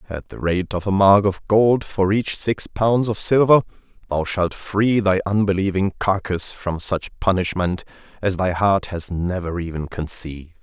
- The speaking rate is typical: Yes, average, 170 wpm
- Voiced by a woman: No, male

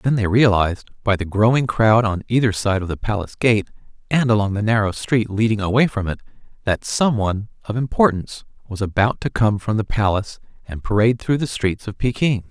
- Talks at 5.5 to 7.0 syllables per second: Yes, 5.8 syllables/s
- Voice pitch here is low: Yes, low, 110 Hz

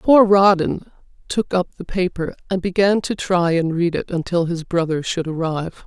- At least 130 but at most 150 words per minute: No, average, 185 wpm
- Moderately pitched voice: Yes, medium, 180 Hz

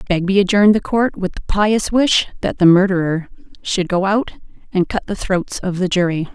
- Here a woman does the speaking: Yes, female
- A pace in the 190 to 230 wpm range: Yes, average, 200 wpm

